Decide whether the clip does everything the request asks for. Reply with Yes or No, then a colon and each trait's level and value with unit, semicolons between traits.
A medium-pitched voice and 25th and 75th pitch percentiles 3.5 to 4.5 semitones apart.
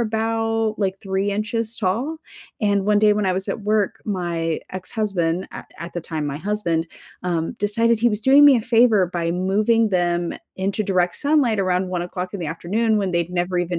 No: high, 195 Hz; average, 3.8 semitones